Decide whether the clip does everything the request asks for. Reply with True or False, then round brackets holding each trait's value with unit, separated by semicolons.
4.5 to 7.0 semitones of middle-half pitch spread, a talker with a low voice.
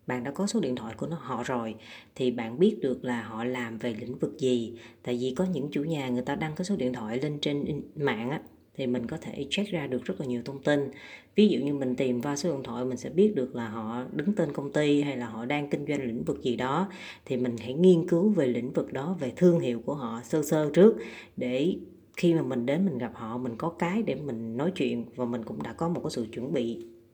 True (5.3 semitones; 130 Hz)